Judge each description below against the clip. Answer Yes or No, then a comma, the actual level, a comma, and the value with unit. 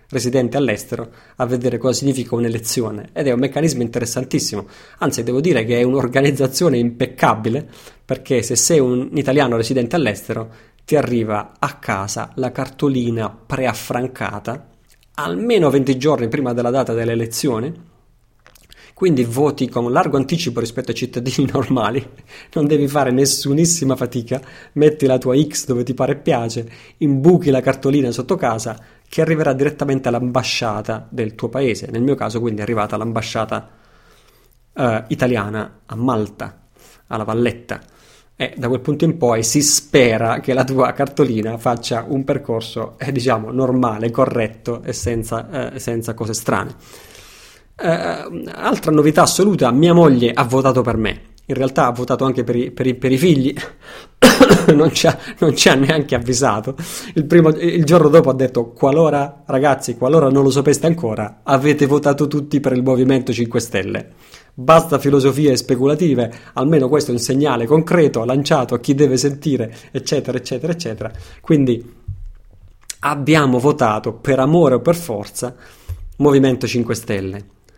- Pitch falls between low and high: No, low, 130 Hz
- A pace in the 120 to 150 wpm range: Yes, average, 145 wpm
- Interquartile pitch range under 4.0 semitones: Yes, average, 3.5 semitones